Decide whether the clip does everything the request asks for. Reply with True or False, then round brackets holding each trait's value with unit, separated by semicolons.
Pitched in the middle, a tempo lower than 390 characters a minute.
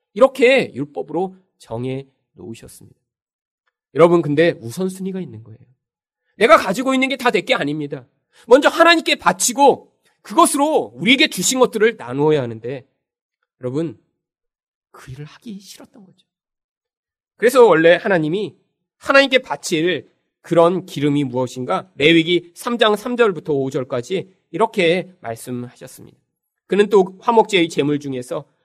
True (180 Hz; 300 characters per minute)